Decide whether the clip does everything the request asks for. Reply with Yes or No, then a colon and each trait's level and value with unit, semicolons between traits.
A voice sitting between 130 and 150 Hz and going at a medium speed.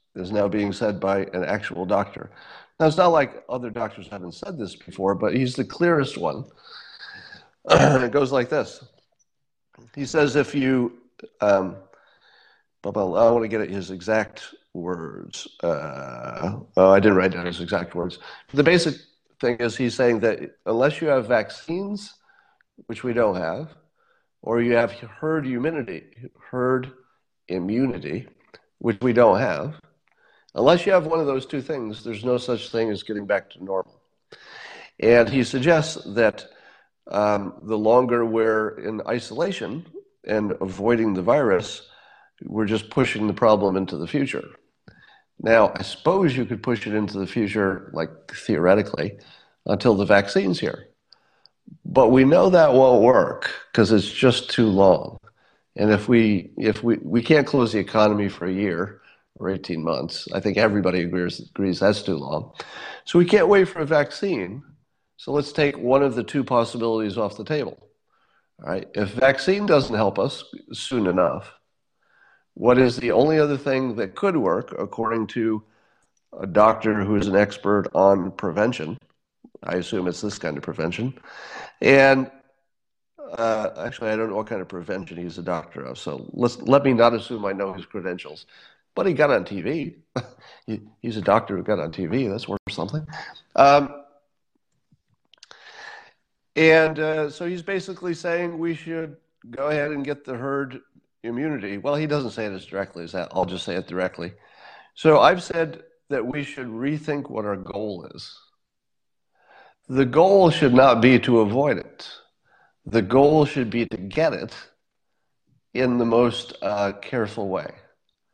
No: low, 120 Hz; average, 165 wpm